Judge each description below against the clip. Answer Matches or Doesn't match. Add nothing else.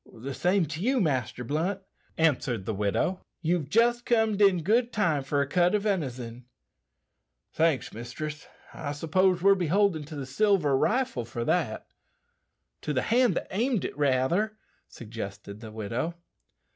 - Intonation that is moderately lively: Doesn't match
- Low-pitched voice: Doesn't match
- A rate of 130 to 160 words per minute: Matches